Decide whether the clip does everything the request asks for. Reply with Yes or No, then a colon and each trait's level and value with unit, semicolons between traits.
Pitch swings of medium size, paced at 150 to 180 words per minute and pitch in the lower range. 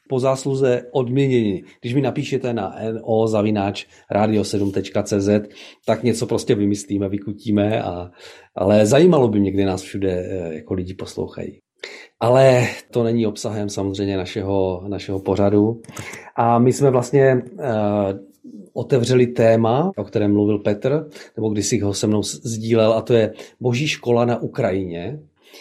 No: average, 3.6 semitones; average, 135 wpm; low, 110 Hz